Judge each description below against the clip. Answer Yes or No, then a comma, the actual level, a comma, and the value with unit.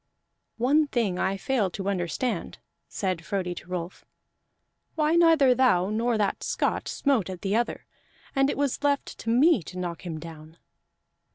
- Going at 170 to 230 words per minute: No, average, 160 wpm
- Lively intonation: Yes, wide, 6.9 semitones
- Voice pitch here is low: No, high, 210 Hz